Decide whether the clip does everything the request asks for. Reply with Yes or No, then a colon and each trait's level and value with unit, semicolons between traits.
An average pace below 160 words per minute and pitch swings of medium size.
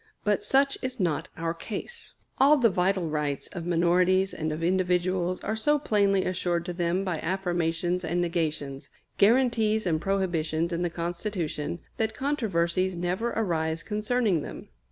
Yes: average, 150 wpm; average, 3.7 semitones